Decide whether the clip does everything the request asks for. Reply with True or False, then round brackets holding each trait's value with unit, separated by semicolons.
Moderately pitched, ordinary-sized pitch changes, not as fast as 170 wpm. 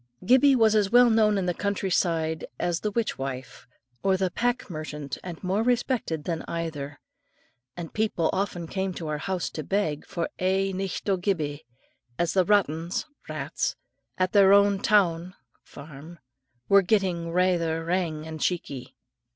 True (180 Hz; 3.6 semitones; 155 wpm)